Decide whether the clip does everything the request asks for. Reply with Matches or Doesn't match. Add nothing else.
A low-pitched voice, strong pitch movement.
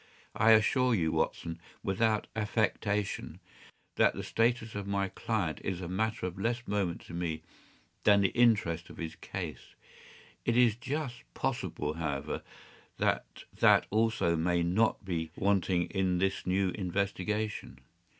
Doesn't match